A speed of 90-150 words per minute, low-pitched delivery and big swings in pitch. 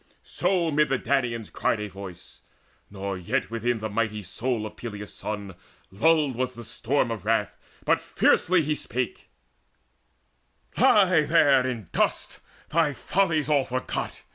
Yes: average, 140 wpm; low, 120 Hz; wide, 5.7 semitones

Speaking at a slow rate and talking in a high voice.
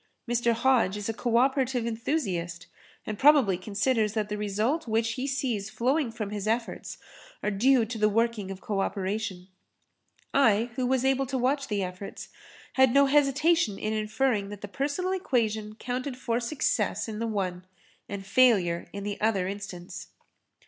No: average, 165 wpm; high, 225 Hz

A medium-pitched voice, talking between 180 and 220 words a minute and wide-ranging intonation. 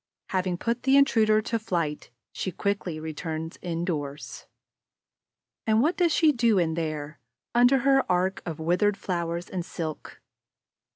No: medium, 180 Hz; slow, 135 wpm; wide, 5.7 semitones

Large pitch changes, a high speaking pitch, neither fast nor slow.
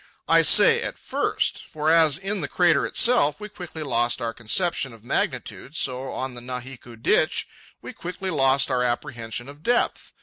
No: wide, 6.0 semitones; medium, 140 Hz; average, 170 wpm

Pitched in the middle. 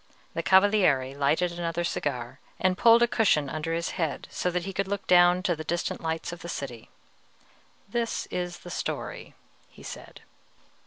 Yes: medium, 175 Hz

